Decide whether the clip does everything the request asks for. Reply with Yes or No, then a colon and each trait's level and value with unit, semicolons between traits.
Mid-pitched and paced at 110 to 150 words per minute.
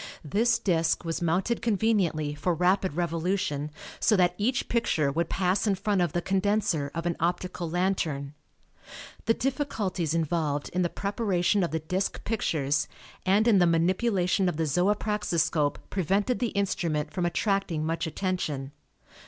Yes: medium, 180 Hz; average, 145 wpm